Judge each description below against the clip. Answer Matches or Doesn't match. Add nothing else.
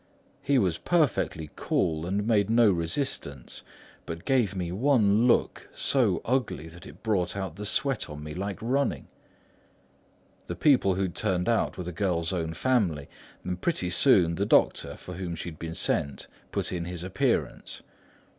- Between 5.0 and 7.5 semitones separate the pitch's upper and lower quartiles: Matches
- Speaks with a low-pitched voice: Matches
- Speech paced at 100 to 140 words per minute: Doesn't match